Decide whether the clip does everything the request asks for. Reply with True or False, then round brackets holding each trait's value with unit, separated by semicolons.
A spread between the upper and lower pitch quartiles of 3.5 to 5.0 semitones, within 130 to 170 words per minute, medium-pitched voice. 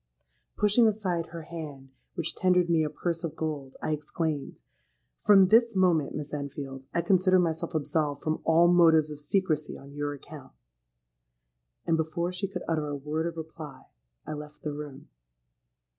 False (3.1 semitones; 160 wpm; 155 Hz)